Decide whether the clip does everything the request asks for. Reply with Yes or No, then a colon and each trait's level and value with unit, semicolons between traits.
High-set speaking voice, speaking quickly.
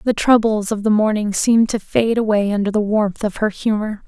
Yes: high, 215 Hz; fast, 220 wpm